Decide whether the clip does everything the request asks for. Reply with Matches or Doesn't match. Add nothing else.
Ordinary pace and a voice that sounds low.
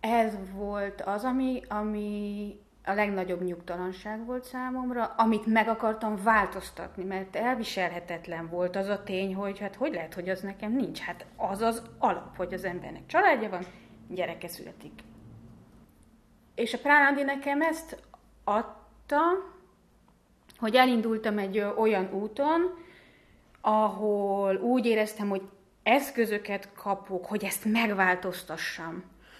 Doesn't match